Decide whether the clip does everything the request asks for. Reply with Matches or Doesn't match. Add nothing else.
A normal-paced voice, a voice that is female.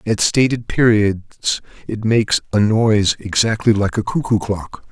Doesn't match